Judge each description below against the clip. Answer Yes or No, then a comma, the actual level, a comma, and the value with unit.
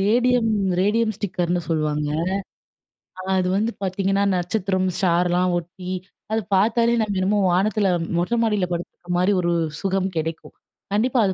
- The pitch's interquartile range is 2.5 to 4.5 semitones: Yes, average, 3.2 semitones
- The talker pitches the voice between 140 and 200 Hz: Yes, high, 190 Hz